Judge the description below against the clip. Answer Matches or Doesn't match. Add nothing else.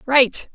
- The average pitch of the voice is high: Matches